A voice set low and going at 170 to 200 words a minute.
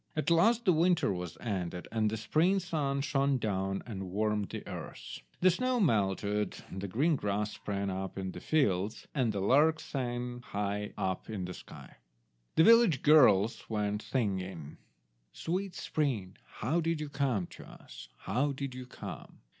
No: low, 120 Hz; average, 160 wpm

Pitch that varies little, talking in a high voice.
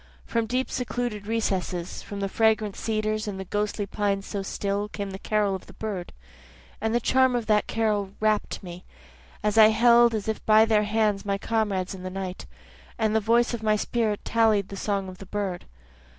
Yes: narrow, 2.0 semitones; high, 210 Hz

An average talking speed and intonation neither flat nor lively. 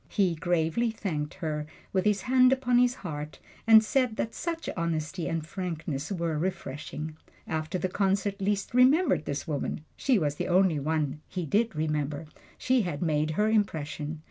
No: average, 165 wpm; wide, 5.7 semitones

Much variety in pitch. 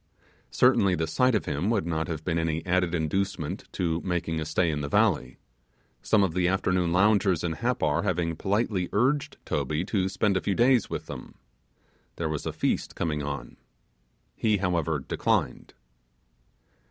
No: average, 3.6 semitones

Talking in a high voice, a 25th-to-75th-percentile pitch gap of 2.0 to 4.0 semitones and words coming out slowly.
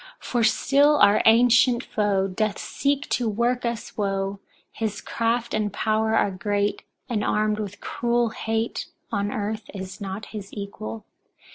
No: high, 215 Hz; average, 2.7 semitones; average, 145 wpm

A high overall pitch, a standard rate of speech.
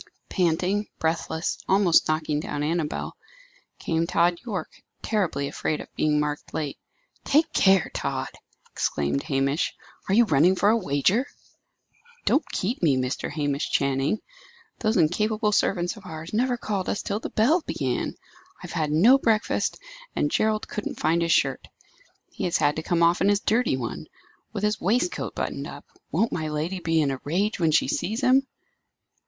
No: medium, 170 Hz; average, 165 wpm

